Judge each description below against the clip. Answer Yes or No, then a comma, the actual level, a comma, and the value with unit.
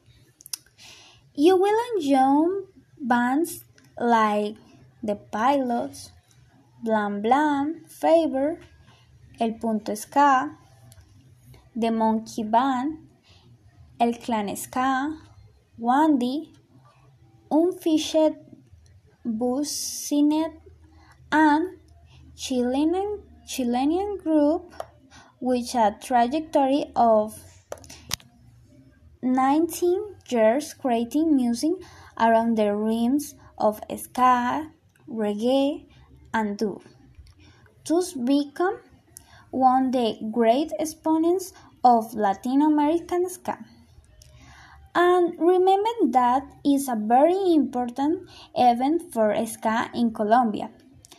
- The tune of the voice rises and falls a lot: Yes, wide, 5.8 semitones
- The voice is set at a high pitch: Yes, very high, 255 Hz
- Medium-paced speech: No, slow, 75 wpm